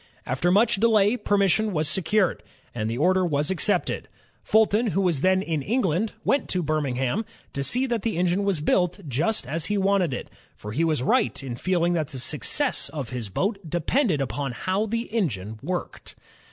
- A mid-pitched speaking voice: Yes, medium, 180 Hz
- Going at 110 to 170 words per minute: No, average, 185 wpm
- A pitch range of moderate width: No, wide, 6.2 semitones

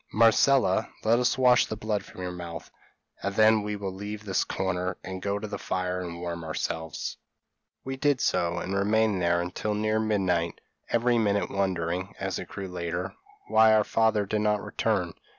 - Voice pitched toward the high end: No, low, 100 Hz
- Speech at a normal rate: Yes, average, 180 wpm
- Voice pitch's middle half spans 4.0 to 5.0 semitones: No, average, 3.3 semitones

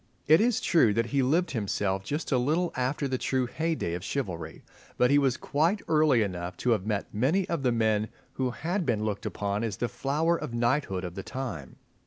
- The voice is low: Yes, low, 125 Hz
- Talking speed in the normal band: No, fast, 210 wpm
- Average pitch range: No, wide, 6.3 semitones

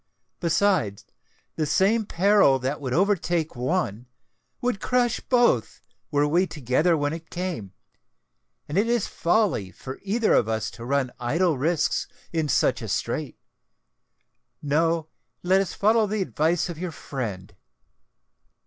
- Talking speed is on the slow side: Yes, slow, 130 wpm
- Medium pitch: Yes, medium, 165 Hz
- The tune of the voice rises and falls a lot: Yes, wide, 6.5 semitones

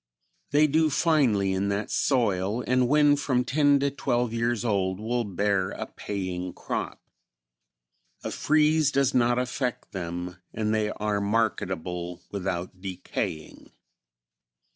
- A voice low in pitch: Yes, low, 110 Hz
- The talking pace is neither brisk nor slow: No, slow, 125 wpm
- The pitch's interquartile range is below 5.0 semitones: No, wide, 5.4 semitones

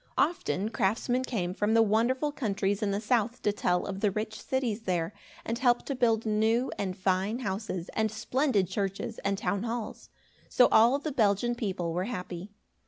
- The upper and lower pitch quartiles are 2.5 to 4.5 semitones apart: Yes, average, 3.6 semitones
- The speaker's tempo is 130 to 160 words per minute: No, average, 175 wpm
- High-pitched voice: Yes, high, 215 Hz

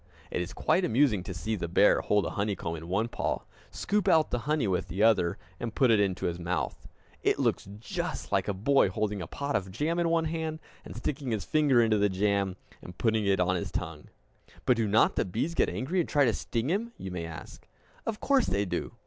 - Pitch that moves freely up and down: Yes, wide, 7.3 semitones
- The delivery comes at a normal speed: No, fast, 230 wpm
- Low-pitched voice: Yes, low, 110 Hz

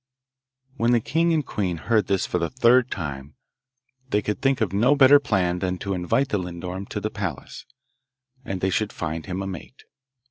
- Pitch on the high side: No, low, 100 Hz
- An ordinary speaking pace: Yes, average, 190 wpm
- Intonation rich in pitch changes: Yes, wide, 5.7 semitones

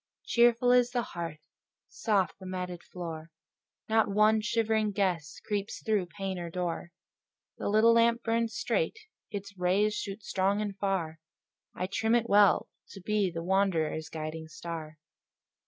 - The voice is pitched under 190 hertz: No, high, 195 Hz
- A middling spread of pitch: Yes, average, 4.0 semitones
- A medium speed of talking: Yes, average, 145 wpm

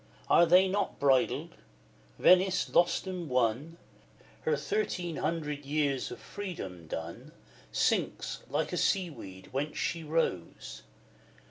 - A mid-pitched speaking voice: Yes, medium, 160 Hz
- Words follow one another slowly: Yes, slow, 120 wpm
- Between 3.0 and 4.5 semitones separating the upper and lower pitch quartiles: No, wide, 5.5 semitones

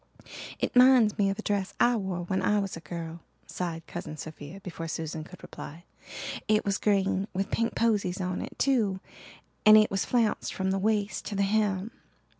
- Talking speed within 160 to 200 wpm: Yes, average, 190 wpm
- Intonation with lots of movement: No, average, 3.0 semitones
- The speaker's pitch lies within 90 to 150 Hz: No, high, 195 Hz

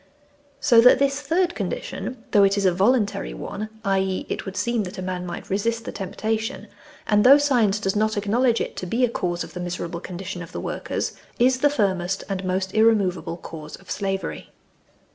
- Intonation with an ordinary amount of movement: Yes, average, 3.9 semitones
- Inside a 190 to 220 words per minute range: Yes, average, 195 wpm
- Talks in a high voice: Yes, high, 200 Hz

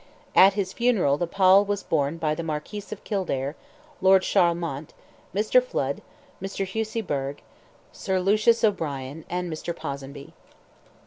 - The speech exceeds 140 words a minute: No, slow, 135 wpm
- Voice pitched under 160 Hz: No, medium, 180 Hz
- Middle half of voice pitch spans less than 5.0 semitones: No, average, 5.3 semitones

